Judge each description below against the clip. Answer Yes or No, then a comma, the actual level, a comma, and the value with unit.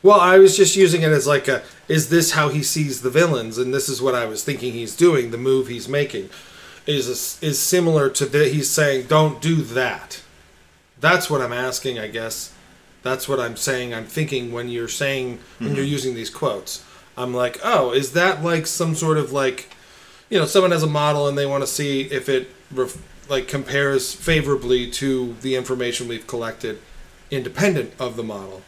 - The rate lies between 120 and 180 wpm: No, average, 195 wpm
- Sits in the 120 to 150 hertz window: Yes, low, 135 Hz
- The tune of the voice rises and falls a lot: No, average, 3.4 semitones